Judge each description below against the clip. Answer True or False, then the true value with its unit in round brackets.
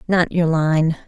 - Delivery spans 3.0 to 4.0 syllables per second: True (3.6 syllables/s)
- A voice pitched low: False (165 Hz)